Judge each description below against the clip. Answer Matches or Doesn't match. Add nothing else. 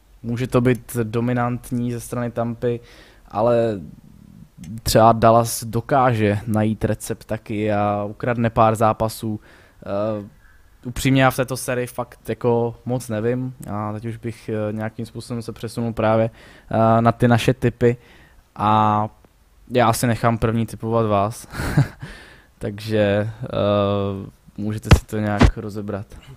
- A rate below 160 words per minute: Matches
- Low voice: Matches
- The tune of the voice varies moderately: Doesn't match